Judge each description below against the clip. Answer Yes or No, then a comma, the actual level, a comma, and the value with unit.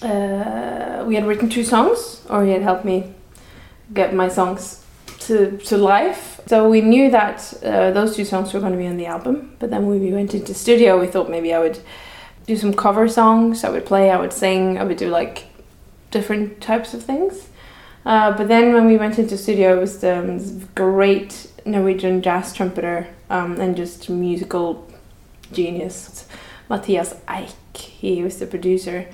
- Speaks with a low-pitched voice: No, high, 195 Hz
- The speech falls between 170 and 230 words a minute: Yes, average, 180 wpm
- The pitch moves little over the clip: No, average, 3.1 semitones